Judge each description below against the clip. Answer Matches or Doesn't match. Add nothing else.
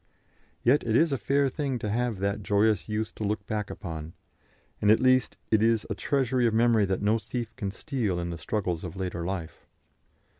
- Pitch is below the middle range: Matches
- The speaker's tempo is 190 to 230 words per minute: Matches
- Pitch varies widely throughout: Doesn't match